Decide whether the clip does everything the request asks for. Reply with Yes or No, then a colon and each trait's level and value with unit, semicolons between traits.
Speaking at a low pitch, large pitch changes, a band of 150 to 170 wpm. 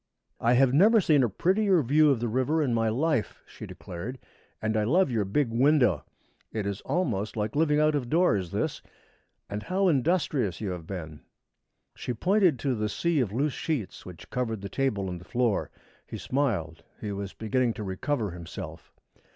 No: low, 120 Hz; wide, 6.5 semitones; average, 185 wpm